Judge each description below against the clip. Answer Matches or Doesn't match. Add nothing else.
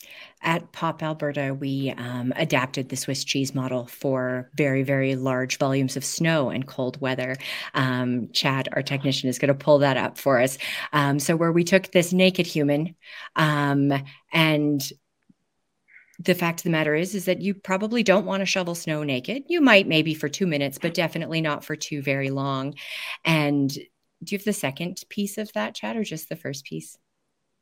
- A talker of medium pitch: Matches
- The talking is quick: Doesn't match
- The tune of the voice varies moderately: Matches